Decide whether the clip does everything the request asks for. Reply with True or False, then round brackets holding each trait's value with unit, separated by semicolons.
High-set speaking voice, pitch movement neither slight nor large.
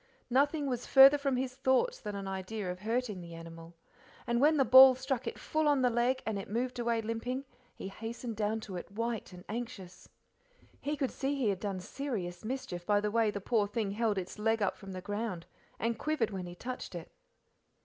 True (225 Hz; 4.7 semitones)